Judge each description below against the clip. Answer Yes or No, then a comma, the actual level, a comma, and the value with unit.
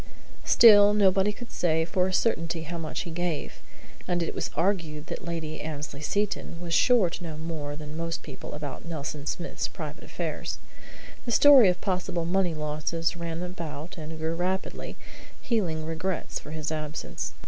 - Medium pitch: Yes, medium, 165 Hz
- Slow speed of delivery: No, average, 165 wpm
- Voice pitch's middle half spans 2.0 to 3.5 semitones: Yes, average, 2.9 semitones